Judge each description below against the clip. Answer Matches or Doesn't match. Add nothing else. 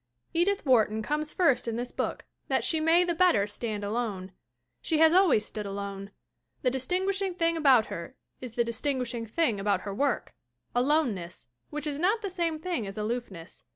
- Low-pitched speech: Doesn't match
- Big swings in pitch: Matches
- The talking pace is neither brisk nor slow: Matches